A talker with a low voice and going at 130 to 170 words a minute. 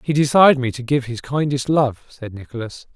No: low, 130 Hz; fast, 205 wpm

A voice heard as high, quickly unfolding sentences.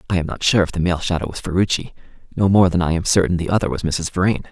No: very low, 90 Hz; fast, 280 wpm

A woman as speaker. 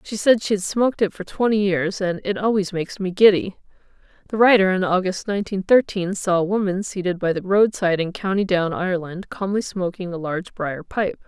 Yes: female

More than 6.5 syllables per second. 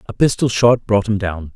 No: 5.0 syllables/s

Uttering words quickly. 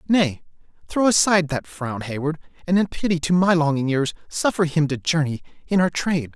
No: average, 190 wpm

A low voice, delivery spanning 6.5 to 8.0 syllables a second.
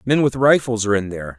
Yes: low, 110 Hz; 7.1 syllables/s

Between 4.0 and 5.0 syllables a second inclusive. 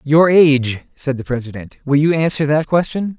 No: 5.2 syllables/s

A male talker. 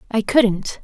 No: female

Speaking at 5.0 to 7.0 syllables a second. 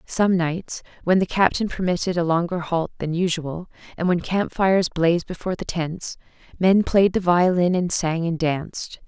No: 4.8 syllables/s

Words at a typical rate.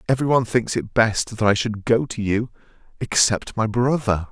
Yes: average, 195 wpm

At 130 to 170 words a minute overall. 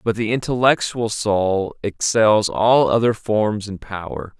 Yes: slow, 135 wpm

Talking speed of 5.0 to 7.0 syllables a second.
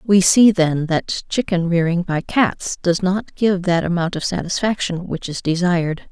No: 4.4 syllables/s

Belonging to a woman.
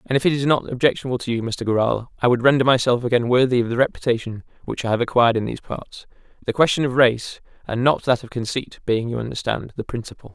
No: male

